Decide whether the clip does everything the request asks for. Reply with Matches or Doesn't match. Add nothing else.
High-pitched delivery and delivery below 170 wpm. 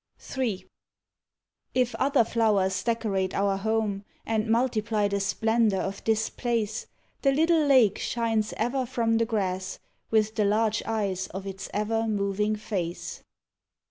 Matches